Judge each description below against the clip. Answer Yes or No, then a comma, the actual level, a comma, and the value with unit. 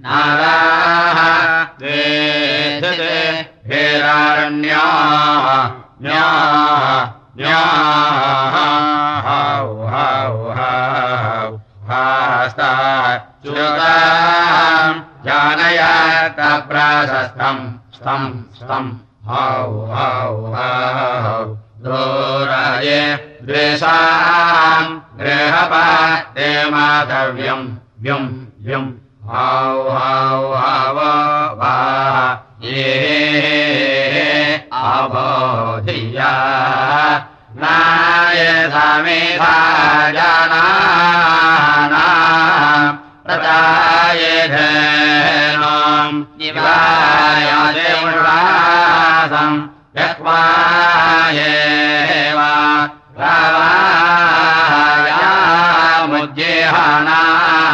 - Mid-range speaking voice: Yes, medium, 150 Hz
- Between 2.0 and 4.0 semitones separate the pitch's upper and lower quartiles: Yes, average, 3.5 semitones